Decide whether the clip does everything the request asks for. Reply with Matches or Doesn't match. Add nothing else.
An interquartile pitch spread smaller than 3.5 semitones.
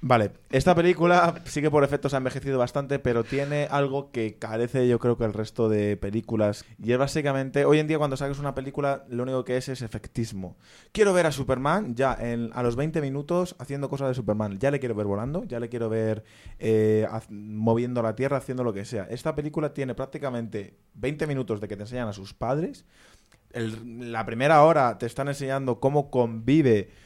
Doesn't match